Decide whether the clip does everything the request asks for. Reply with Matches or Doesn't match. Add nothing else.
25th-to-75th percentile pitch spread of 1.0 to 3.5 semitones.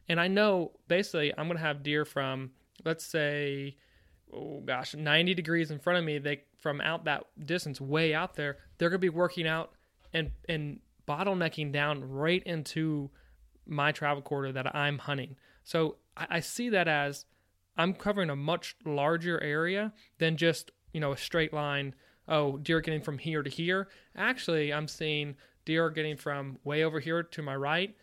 Matches